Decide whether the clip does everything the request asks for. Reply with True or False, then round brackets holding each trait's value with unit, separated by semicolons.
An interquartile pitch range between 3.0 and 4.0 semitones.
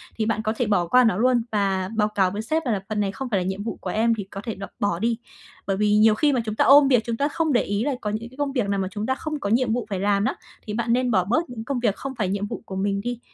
True (3.6 semitones)